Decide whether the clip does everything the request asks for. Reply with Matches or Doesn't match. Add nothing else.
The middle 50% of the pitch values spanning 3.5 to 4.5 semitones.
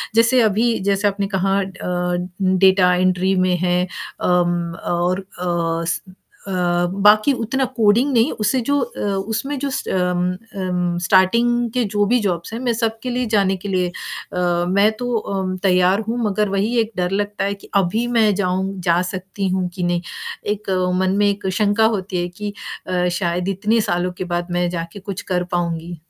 Doesn't match